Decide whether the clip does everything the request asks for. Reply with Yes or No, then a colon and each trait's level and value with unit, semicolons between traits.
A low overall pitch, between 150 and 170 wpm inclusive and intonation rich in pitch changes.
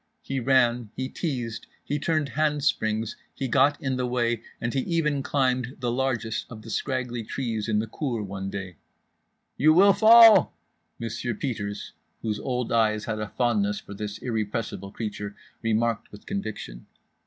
No: low, 120 Hz; average, 155 wpm; average, 3.9 semitones